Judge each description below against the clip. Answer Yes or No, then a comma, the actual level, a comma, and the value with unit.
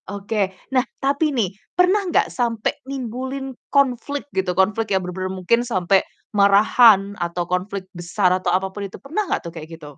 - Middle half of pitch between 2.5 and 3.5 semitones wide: No, wide, 5.4 semitones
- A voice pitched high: Yes, high, 200 Hz